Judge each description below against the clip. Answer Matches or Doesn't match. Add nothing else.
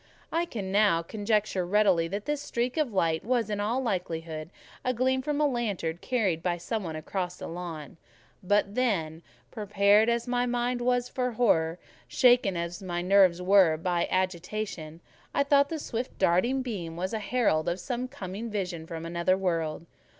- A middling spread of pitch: Doesn't match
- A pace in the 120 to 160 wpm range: Doesn't match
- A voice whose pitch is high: Matches